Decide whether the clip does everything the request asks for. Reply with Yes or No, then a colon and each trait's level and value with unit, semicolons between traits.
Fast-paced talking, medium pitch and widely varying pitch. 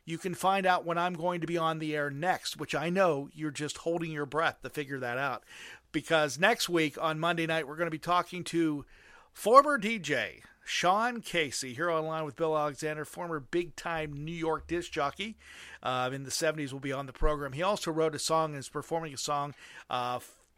No: fast, 215 wpm; medium, 160 Hz; average, 2.9 semitones